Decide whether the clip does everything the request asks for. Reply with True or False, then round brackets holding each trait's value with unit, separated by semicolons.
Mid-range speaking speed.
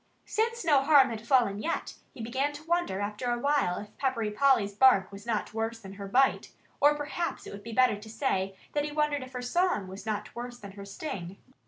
False (225 wpm)